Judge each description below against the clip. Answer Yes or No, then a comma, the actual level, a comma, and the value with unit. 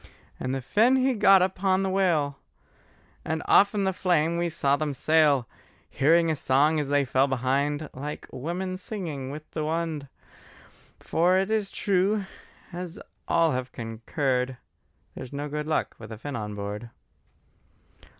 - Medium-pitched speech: Yes, medium, 155 Hz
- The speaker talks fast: No, average, 155 wpm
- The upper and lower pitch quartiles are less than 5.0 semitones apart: No, average, 5.3 semitones